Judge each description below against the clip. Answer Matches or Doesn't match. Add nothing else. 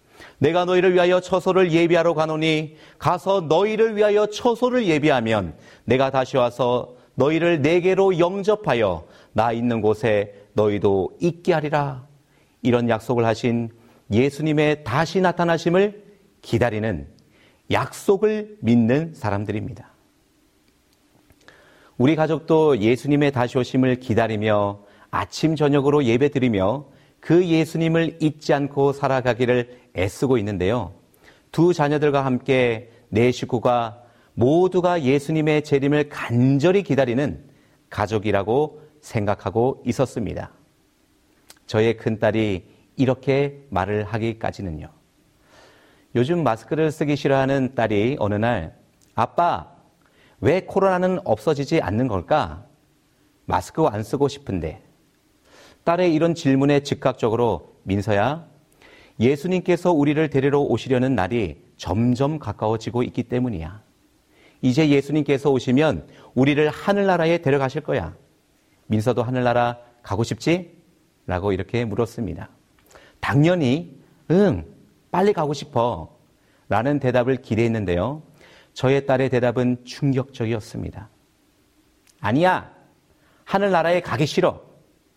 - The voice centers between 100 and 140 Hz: Matches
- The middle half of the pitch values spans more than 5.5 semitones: Doesn't match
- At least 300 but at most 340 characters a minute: Doesn't match